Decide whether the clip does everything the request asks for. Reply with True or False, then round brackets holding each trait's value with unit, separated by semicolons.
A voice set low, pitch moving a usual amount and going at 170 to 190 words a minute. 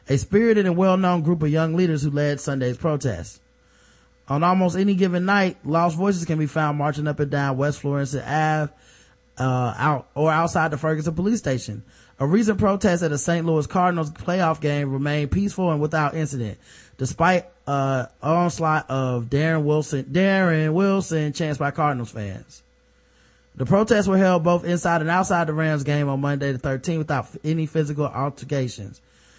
False (150 Hz; 4.1 semitones; 175 wpm)